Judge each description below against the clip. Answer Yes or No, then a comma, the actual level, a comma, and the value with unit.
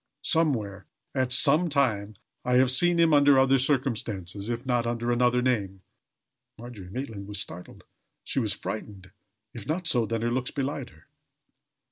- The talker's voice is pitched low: Yes, low, 120 Hz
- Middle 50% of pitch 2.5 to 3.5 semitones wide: No, average, 4.3 semitones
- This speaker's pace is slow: No, average, 155 wpm